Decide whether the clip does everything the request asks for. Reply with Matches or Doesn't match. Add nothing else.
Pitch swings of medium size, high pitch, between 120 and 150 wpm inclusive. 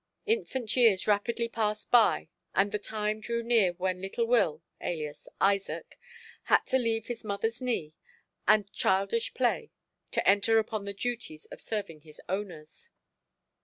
Matches